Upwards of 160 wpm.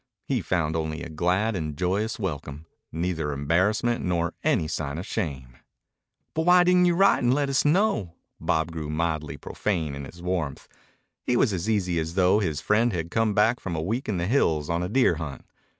Yes: average, 200 wpm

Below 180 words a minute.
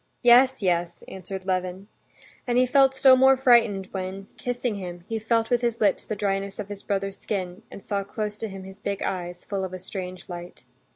No: fast, 205 wpm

